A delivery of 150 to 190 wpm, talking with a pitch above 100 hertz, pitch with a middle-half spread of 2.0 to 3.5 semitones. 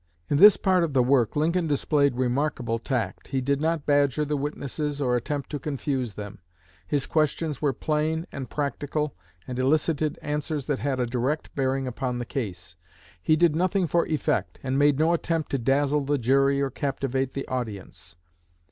Yes: average, 175 wpm; medium, 140 Hz; average, 2.8 semitones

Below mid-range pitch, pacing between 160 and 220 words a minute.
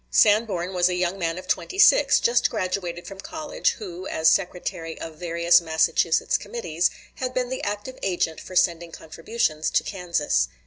No: medium, 180 Hz; average, 165 wpm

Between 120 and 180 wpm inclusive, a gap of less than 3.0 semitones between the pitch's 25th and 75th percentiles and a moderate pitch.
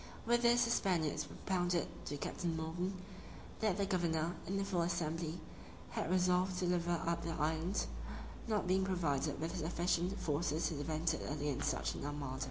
Yes: average, 170 wpm; narrow, 2.6 semitones; medium, 170 Hz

